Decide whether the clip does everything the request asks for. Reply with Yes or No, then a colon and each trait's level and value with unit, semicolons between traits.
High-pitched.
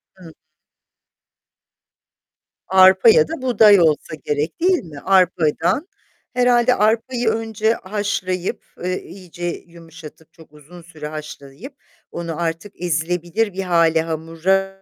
No: medium, 180 Hz